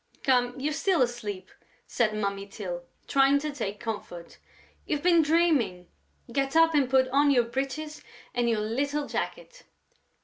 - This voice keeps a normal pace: Yes, average, 145 wpm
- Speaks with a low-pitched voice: No, very high, 265 Hz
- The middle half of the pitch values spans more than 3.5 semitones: Yes, wide, 5.6 semitones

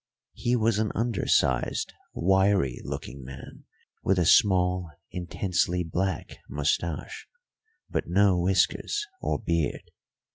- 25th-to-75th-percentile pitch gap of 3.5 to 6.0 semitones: No, average, 3.1 semitones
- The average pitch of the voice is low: Yes, very low, 90 Hz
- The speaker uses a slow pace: Yes, slow, 105 wpm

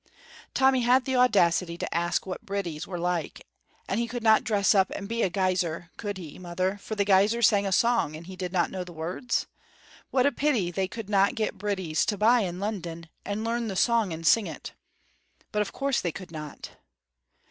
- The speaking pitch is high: Yes, high, 195 Hz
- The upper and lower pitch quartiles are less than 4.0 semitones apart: No, average, 4.3 semitones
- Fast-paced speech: Yes, fast, 210 wpm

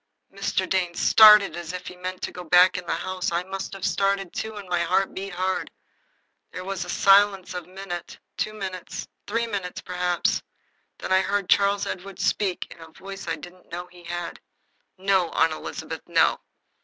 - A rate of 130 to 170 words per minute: No, average, 185 wpm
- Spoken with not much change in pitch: Yes, narrow, 1.7 semitones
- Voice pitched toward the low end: No, medium, 185 Hz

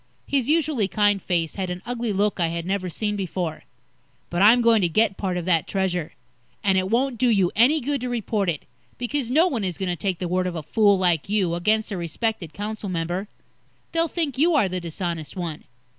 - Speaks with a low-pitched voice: No, high, 195 Hz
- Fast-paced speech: Yes, fast, 220 wpm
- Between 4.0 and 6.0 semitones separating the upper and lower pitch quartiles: Yes, average, 4.7 semitones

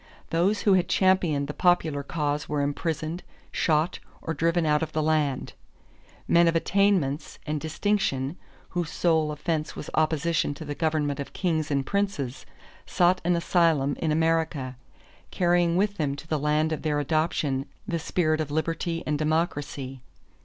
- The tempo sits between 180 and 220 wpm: No, average, 155 wpm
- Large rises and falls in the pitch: No, narrow, 2.5 semitones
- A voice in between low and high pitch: Yes, medium, 155 Hz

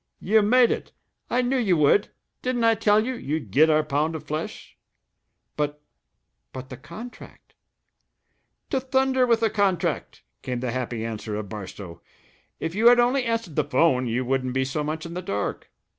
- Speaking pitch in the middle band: Yes, medium, 160 Hz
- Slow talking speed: No, average, 180 wpm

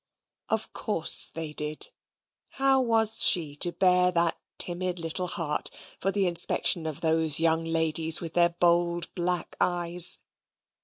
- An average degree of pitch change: No, narrow, 1.9 semitones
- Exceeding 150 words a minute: No, average, 140 wpm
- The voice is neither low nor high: Yes, medium, 170 Hz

